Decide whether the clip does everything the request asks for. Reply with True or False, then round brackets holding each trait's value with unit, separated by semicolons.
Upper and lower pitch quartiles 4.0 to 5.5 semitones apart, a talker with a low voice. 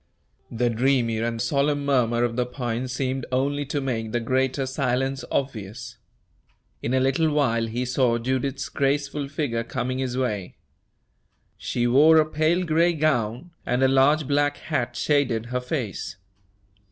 False (2.9 semitones; 130 Hz)